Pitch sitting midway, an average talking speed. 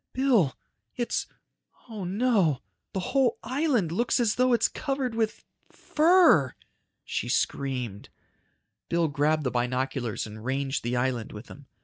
No: medium, 165 Hz; slow, 130 wpm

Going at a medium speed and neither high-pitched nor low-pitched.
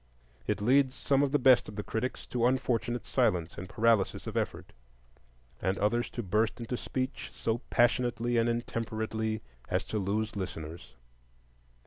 No: average, 150 wpm; low, 115 Hz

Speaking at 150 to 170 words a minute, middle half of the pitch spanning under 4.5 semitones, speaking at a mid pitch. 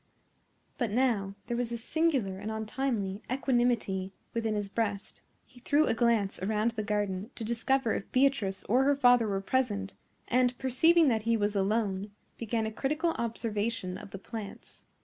No: average, 165 wpm; average, 3.4 semitones; high, 225 Hz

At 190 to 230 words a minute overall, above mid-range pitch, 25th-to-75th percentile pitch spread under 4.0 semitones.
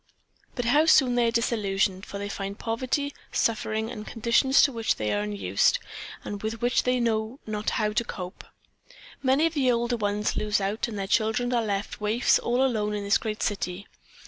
Yes: average, 195 wpm; high, 220 Hz; average, 3.1 semitones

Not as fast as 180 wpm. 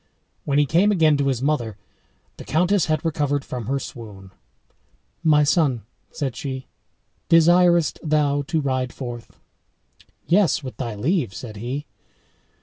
Yes: average, 140 wpm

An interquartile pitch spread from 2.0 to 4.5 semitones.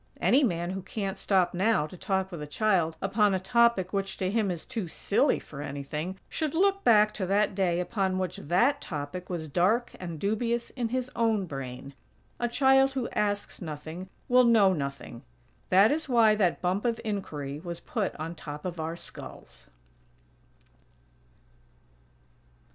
No: average, 4.9 semitones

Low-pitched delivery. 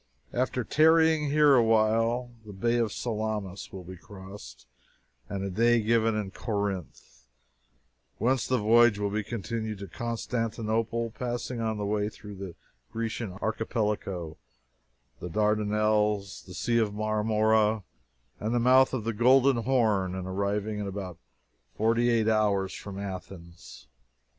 Yes: low, 110 Hz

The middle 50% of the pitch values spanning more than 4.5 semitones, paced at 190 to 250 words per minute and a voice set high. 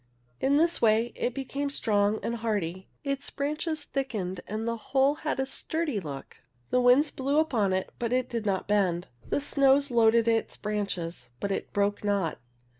No: average, 5.3 semitones; average, 175 wpm; high, 230 Hz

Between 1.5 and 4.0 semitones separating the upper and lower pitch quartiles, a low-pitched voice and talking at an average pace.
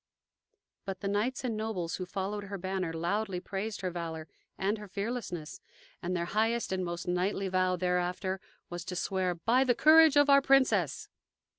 No: average, 3.5 semitones; high, 190 Hz; average, 170 wpm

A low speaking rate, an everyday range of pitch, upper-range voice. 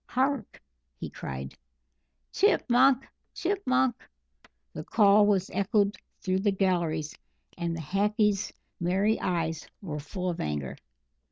Yes: slow, 120 wpm; average, 4.3 semitones; high, 195 Hz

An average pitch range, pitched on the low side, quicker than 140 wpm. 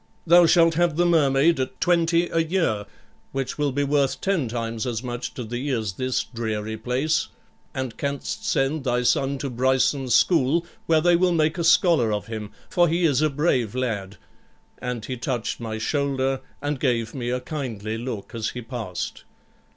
Yes: average, 5.0 semitones; low, 130 Hz; average, 180 wpm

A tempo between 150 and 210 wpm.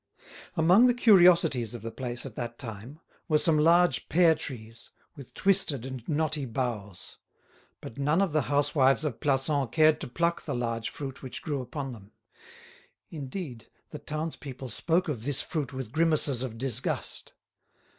Yes: average, 155 wpm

